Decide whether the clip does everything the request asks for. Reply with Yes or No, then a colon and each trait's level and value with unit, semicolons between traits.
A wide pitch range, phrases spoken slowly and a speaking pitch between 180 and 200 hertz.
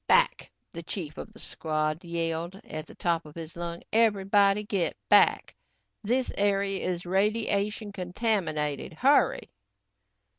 No: average, 3.6 semitones; slow, 125 wpm; high, 190 Hz